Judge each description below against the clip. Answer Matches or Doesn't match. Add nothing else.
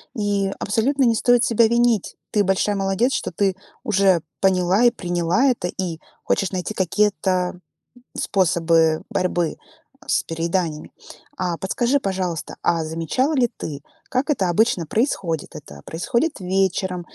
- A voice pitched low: Doesn't match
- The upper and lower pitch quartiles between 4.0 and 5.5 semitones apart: Matches